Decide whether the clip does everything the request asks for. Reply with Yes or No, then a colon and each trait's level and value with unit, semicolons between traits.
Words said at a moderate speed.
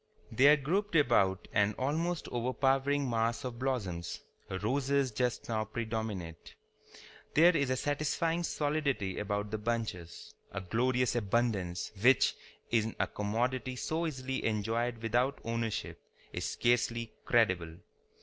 No: slow, 120 wpm